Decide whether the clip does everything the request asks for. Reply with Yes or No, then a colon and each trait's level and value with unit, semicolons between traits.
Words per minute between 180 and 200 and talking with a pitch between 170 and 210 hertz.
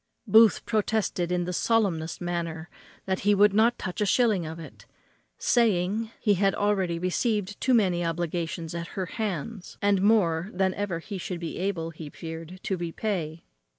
No: average, 165 wpm; medium, 185 Hz